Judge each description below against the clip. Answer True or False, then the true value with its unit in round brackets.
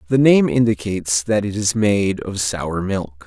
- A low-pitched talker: True (100 Hz)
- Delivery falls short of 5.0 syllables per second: True (4.3 syllables/s)